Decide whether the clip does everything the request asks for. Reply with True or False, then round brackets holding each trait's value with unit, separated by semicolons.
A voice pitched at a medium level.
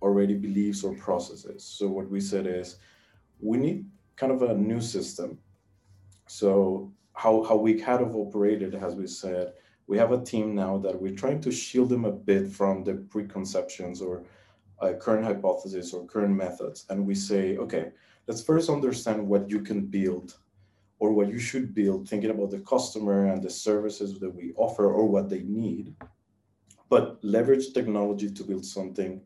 False (100 Hz)